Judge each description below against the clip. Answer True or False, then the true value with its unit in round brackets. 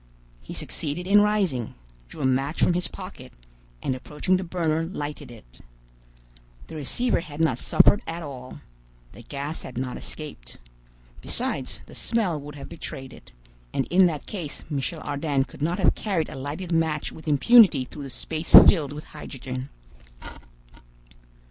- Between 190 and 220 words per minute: False (155 wpm)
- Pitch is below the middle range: False (150 Hz)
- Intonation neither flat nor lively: True (4.3 semitones)